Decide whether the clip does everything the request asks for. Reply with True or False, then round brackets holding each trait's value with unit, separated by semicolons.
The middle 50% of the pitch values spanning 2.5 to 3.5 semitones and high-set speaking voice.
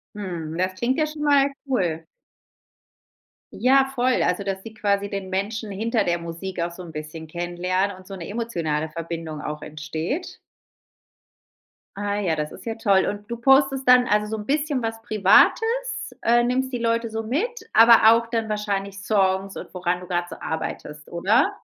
False (5.3 semitones; 205 Hz)